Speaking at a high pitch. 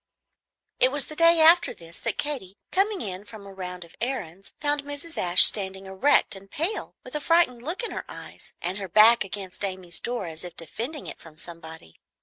Yes: high, 205 Hz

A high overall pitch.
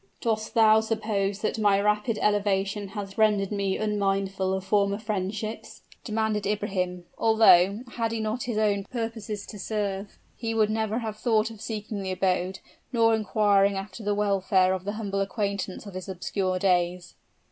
Yes: high, 205 Hz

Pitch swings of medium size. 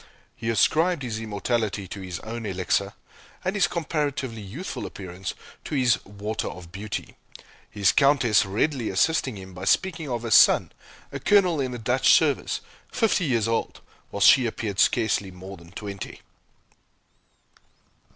No: wide, 5.7 semitones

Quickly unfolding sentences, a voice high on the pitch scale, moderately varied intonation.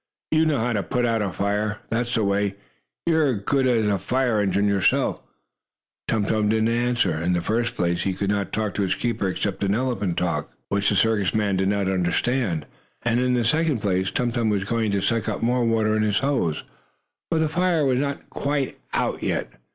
No: fast, 215 wpm; low, 110 Hz; average, 3.7 semitones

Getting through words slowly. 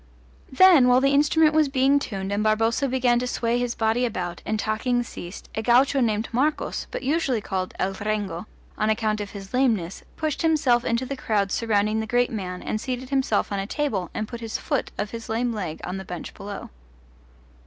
No: average, 200 wpm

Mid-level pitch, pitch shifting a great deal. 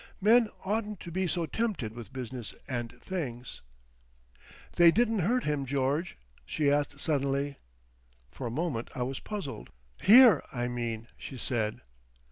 Yes: medium, 145 Hz; wide, 7.3 semitones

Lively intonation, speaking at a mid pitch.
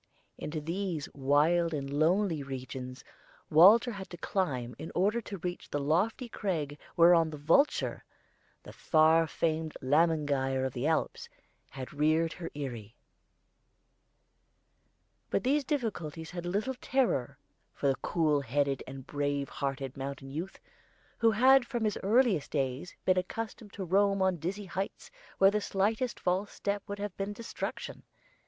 Yes: wide, 5.9 semitones; medium, 165 Hz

